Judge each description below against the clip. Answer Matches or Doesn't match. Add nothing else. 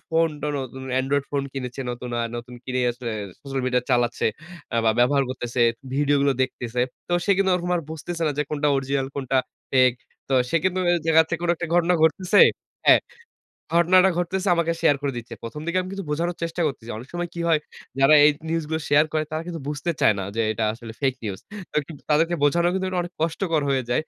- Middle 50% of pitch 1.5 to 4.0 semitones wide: Doesn't match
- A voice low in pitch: Doesn't match